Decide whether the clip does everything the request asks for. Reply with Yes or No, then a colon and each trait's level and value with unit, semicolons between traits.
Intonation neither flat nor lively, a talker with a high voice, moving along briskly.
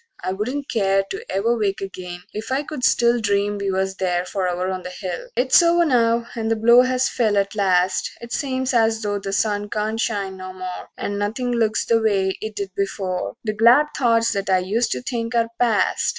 Yes: average, 3.4 semitones; high, 215 Hz; fast, 210 wpm